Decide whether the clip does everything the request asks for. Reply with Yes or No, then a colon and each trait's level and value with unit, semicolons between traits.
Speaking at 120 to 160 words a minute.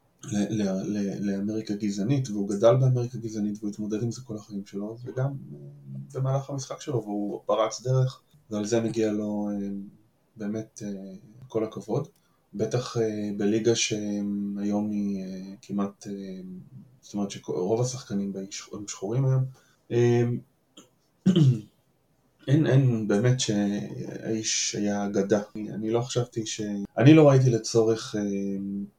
Yes: average, 140 wpm